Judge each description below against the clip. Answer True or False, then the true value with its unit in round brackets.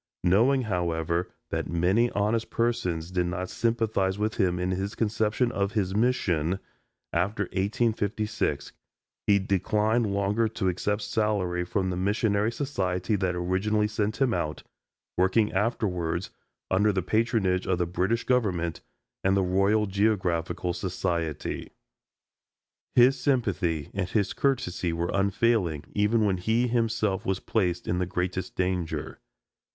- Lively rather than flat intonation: False (3.5 semitones)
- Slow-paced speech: True (130 wpm)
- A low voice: True (100 Hz)